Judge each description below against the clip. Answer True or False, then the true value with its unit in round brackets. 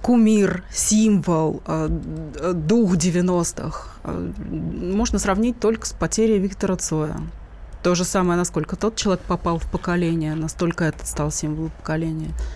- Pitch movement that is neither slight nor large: True (3.6 semitones)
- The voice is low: False (175 Hz)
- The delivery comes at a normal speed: True (120 wpm)